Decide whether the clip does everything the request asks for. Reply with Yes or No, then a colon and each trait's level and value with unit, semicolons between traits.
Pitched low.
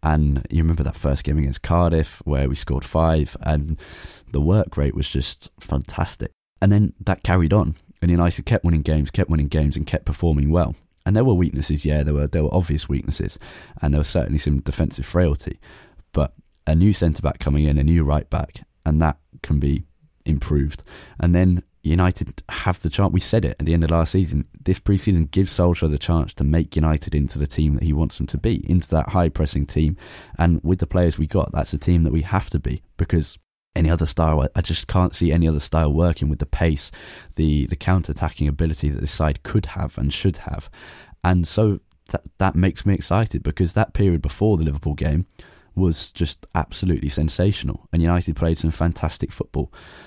Yes: very low, 80 Hz